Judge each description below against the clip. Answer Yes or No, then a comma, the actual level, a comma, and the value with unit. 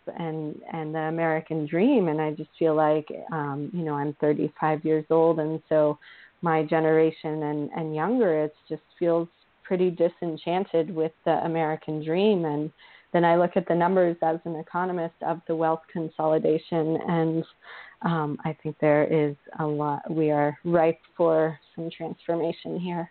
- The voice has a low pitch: No, medium, 160 Hz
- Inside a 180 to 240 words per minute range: No, average, 160 wpm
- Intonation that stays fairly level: Yes, narrow, 1.5 semitones